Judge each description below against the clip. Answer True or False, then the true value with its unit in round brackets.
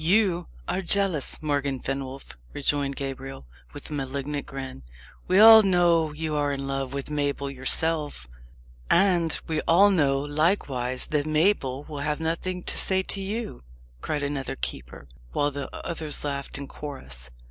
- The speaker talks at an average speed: True (150 wpm)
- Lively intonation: False (3.5 semitones)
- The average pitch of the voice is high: False (145 Hz)